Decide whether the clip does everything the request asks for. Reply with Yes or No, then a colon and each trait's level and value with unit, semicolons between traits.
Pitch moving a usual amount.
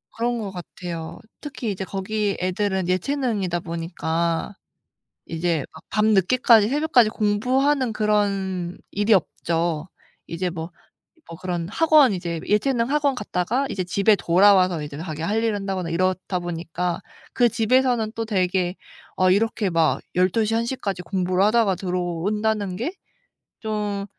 Yes: average, 3.9 semitones